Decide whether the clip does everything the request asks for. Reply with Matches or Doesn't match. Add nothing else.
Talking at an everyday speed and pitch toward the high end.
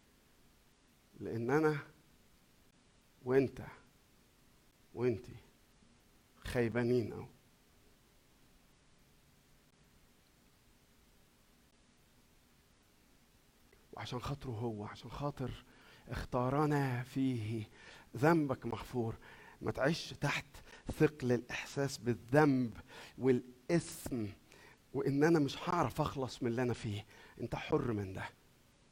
Doesn't match